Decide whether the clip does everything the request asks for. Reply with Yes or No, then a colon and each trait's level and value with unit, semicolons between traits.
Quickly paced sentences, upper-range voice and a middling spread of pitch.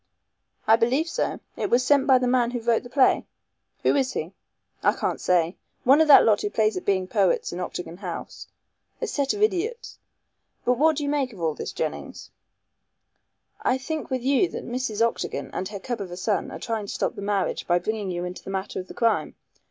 No: fast, 220 wpm; high, 230 Hz; wide, 5.7 semitones